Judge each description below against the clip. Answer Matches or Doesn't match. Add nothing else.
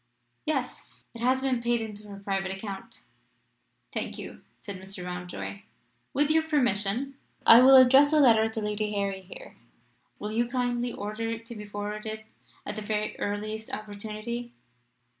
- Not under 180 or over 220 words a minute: Doesn't match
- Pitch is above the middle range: Matches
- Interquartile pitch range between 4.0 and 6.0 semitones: Doesn't match